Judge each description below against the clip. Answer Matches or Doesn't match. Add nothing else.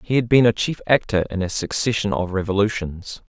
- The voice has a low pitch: Matches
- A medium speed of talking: Matches